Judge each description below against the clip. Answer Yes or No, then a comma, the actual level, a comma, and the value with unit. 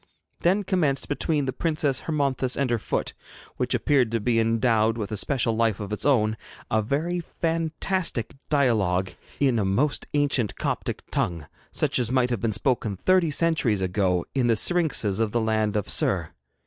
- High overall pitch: No, low, 120 Hz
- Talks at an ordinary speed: Yes, average, 175 wpm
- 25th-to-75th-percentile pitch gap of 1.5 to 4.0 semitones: No, average, 5.2 semitones